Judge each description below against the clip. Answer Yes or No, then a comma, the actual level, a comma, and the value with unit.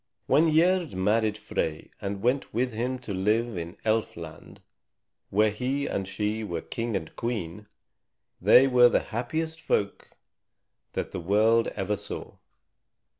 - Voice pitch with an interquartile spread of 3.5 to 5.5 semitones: Yes, average, 4.0 semitones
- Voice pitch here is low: Yes, low, 110 Hz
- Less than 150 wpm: Yes, average, 140 wpm